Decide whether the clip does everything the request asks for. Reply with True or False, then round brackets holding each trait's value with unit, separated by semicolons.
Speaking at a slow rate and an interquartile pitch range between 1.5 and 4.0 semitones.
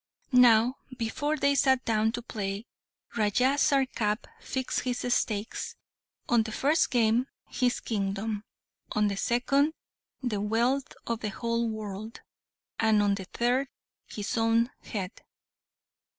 True (125 wpm; 3.0 semitones)